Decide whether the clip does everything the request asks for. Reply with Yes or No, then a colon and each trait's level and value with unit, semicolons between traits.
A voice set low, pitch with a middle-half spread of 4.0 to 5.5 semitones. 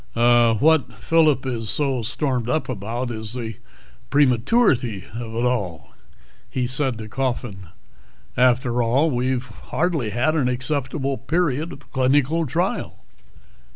No: low, 125 Hz; average, 3.3 semitones